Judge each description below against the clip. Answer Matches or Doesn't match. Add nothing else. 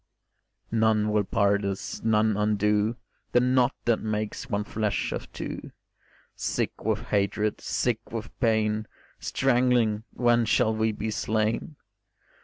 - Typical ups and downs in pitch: Doesn't match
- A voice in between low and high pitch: Doesn't match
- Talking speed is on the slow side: Matches